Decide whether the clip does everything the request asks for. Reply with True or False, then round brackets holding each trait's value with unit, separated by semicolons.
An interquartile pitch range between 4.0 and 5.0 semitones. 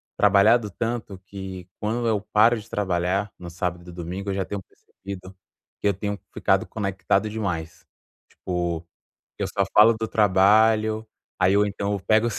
False (2.7 semitones)